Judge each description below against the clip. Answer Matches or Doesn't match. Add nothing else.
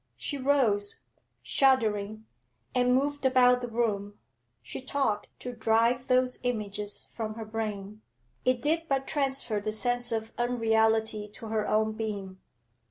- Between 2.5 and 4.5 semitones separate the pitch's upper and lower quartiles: Matches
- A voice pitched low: Doesn't match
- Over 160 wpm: Doesn't match